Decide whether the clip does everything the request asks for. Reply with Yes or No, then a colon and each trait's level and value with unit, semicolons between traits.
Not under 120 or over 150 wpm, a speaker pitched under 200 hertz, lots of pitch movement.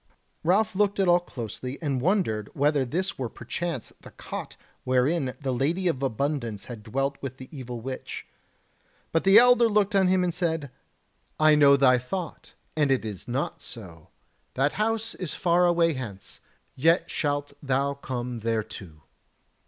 No: average, 160 wpm; medium, 140 Hz; wide, 5.7 semitones